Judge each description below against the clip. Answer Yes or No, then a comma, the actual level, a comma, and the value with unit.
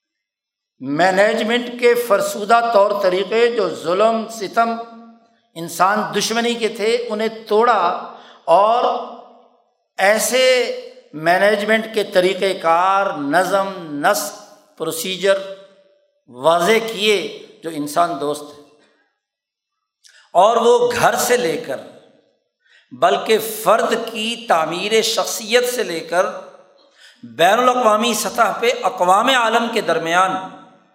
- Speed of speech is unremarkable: No, slow, 100 wpm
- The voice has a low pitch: No, high, 220 Hz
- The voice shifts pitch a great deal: No, average, 4.2 semitones